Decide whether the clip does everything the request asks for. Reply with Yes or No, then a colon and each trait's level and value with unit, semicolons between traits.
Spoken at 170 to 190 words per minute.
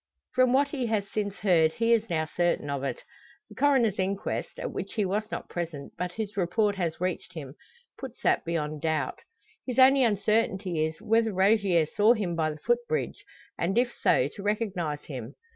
Yes: average, 185 wpm